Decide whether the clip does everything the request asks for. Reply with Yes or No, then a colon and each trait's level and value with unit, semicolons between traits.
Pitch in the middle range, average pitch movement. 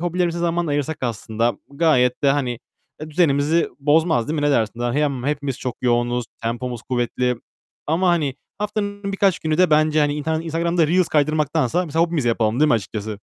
Yes: medium, 150 Hz; average, 5.0 semitones